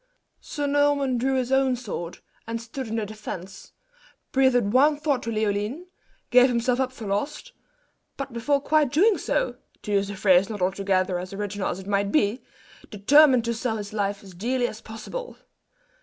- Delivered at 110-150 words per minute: No, average, 175 wpm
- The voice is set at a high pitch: Yes, high, 230 Hz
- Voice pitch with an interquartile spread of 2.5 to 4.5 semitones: No, average, 4.9 semitones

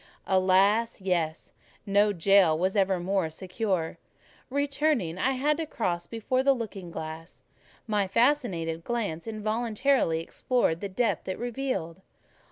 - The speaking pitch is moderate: No, high, 200 Hz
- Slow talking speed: Yes, slow, 125 wpm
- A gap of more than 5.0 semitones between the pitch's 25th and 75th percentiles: Yes, wide, 5.5 semitones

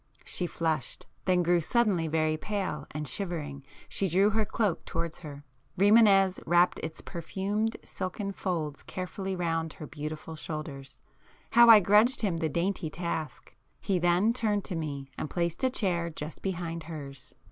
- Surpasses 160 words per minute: No, average, 155 wpm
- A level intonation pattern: No, average, 4.0 semitones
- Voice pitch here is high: No, medium, 175 Hz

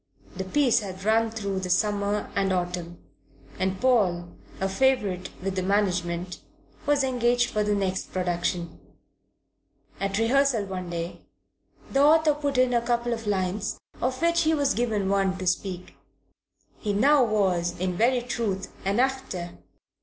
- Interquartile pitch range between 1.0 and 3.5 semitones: No, average, 4.7 semitones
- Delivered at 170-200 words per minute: No, average, 150 wpm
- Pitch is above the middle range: Yes, high, 205 Hz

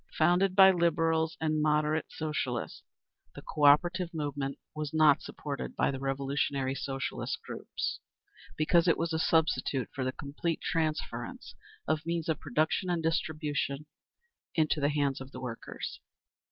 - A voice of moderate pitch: Yes, medium, 155 Hz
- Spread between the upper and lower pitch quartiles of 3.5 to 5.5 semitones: No, narrow, 2.6 semitones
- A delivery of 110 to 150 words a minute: Yes, average, 140 wpm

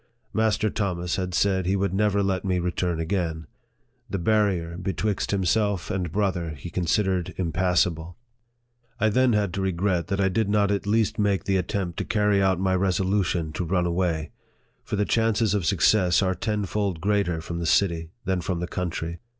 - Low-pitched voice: Yes, very low, 95 Hz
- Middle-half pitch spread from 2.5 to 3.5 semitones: Yes, average, 2.8 semitones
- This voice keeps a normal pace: Yes, average, 175 wpm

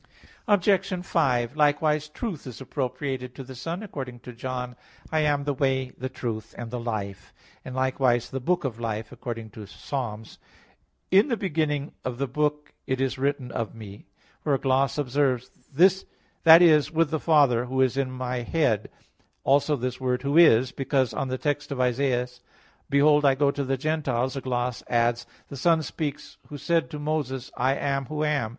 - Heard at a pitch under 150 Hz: Yes, low, 135 Hz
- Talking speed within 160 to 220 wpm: Yes, average, 185 wpm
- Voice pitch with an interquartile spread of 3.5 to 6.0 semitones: No, average, 3.1 semitones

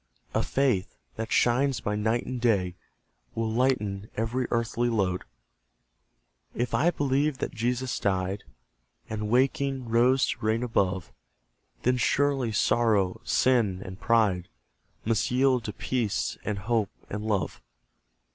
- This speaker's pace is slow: Yes, slow, 130 wpm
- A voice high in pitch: No, low, 115 Hz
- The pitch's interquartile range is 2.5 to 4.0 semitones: Yes, average, 3.6 semitones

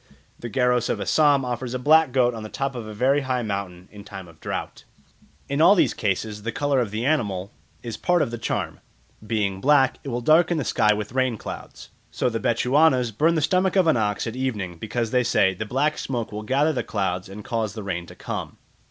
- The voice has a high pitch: No, low, 120 Hz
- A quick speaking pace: Yes, fast, 225 wpm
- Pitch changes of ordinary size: Yes, average, 4.6 semitones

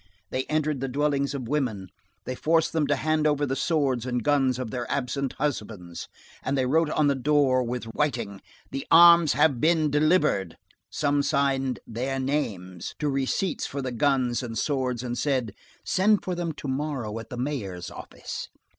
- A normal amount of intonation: Yes, average, 3.4 semitones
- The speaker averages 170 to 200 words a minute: Yes, average, 175 wpm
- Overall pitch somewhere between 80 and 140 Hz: Yes, low, 135 Hz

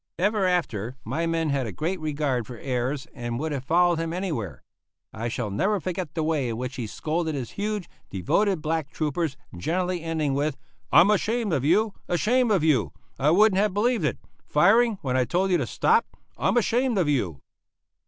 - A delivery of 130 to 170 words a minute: No, average, 190 wpm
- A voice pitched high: No, medium, 160 Hz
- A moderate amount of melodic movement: No, wide, 6.3 semitones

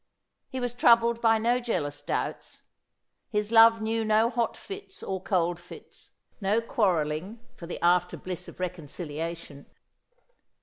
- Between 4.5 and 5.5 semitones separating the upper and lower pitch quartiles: Yes, average, 4.9 semitones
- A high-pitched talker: Yes, high, 210 Hz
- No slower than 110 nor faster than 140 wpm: Yes, slow, 135 wpm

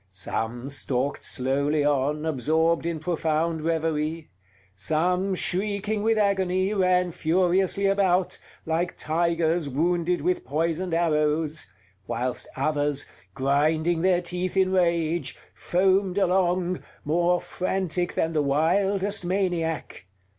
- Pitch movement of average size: Yes, average, 3.1 semitones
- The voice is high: No, medium, 170 Hz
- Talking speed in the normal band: No, slow, 105 wpm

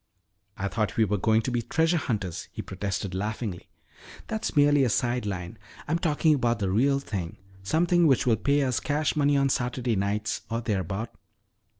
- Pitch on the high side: No, low, 120 Hz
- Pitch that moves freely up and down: Yes, wide, 6.0 semitones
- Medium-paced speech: Yes, average, 180 wpm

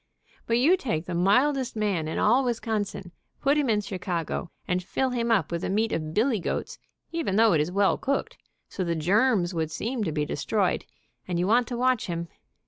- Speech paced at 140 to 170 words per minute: No, fast, 205 wpm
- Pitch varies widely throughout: Yes, wide, 5.7 semitones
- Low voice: No, high, 205 Hz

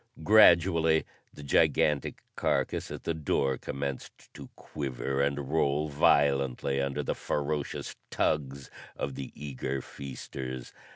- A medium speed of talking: No, slow, 115 wpm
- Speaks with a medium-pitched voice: No, very low, 70 Hz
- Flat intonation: Yes, narrow, 1.8 semitones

